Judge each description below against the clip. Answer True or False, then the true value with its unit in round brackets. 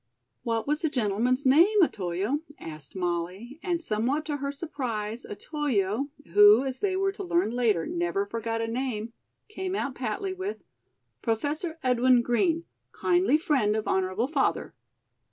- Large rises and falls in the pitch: True (6.6 semitones)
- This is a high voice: True (250 Hz)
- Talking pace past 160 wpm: False (145 wpm)